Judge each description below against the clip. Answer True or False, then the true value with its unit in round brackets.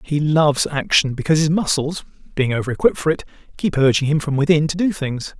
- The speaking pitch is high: False (150 Hz)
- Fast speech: True (210 wpm)